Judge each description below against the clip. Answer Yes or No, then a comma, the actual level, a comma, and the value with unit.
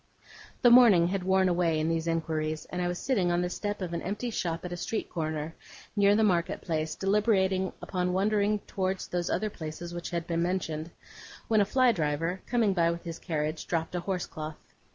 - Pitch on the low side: No, medium, 180 Hz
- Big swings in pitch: No, average, 3.1 semitones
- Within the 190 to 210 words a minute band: Yes, average, 200 wpm